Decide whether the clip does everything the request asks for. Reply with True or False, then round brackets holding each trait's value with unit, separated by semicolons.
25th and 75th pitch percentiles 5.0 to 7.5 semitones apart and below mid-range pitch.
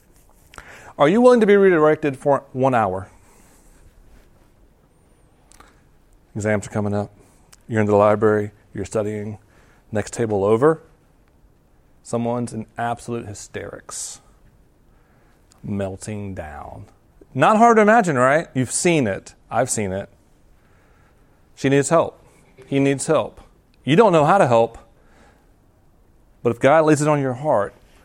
True (5.4 semitones; 115 Hz)